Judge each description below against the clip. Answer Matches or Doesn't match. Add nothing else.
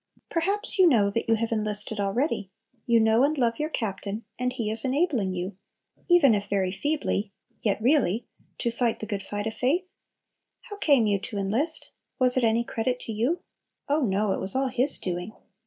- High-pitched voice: Matches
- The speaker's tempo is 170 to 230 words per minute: Matches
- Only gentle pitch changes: Doesn't match